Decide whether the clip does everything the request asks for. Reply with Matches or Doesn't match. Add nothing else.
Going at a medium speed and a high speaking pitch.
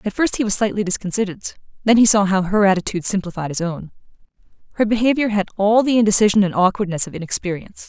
Matches